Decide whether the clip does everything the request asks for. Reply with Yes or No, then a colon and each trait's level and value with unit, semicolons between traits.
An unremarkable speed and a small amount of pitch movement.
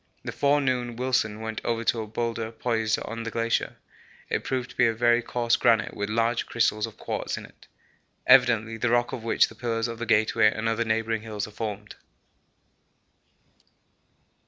Yes: average, 180 wpm; narrow, 1.3 semitones